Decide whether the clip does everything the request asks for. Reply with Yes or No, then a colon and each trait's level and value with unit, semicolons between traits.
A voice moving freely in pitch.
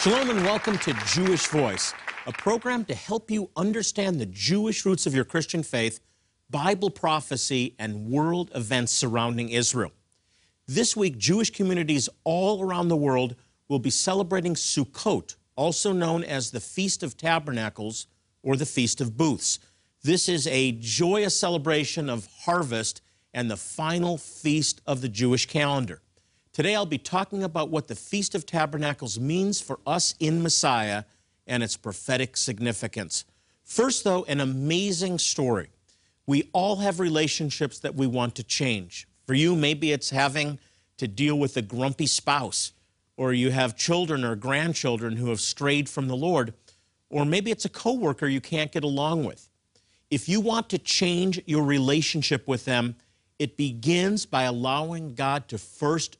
Yes: wide, 6.6 semitones